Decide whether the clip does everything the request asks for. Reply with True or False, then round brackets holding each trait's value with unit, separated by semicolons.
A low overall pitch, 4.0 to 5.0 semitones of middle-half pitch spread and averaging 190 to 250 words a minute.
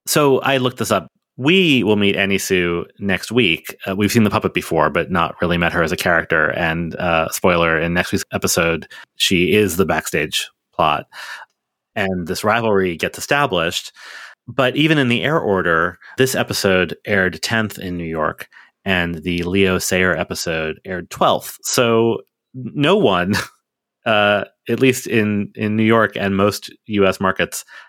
False (100 Hz; 4.3 semitones; 165 wpm)